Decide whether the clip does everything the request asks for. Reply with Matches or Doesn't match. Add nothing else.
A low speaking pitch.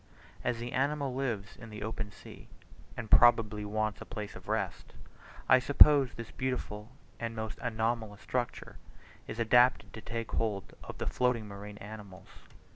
Matches